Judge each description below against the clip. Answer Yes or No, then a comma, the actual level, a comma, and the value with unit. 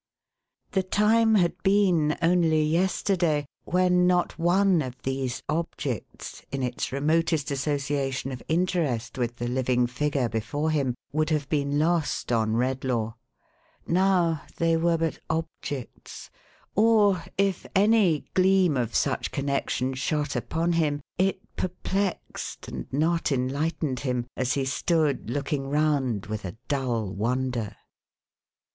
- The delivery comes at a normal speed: No, slow, 125 wpm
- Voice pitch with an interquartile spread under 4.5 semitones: No, average, 4.9 semitones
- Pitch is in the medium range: Yes, medium, 150 Hz